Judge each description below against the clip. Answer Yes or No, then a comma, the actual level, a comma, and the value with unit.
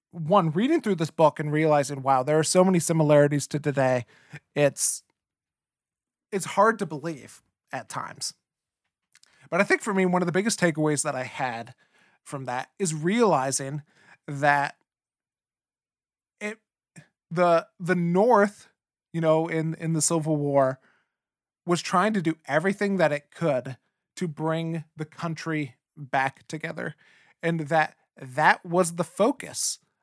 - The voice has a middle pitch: Yes, medium, 160 Hz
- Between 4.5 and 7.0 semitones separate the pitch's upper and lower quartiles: No, average, 3.7 semitones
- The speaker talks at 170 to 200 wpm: No, average, 140 wpm